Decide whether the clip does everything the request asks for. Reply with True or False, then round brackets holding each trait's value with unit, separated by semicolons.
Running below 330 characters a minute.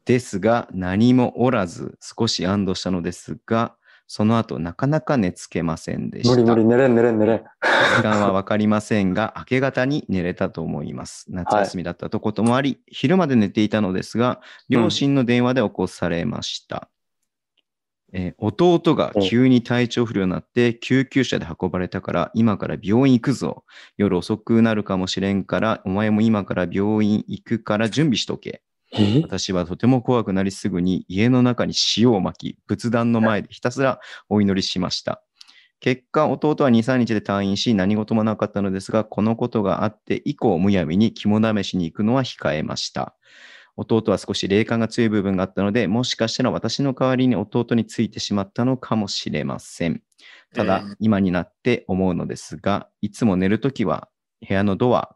False (345 characters per minute)